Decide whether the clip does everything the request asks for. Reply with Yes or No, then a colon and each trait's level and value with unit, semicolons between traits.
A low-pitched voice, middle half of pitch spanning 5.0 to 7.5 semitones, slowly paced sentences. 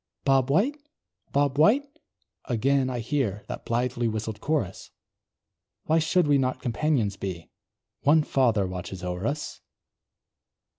Yes: low, 130 Hz; wide, 5.5 semitones; slow, 120 wpm